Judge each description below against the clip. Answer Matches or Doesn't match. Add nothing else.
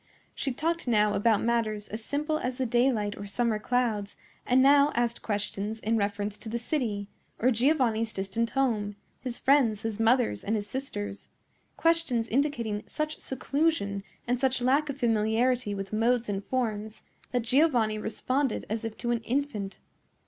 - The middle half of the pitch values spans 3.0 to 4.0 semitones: Matches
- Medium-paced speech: Matches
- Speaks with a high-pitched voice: Matches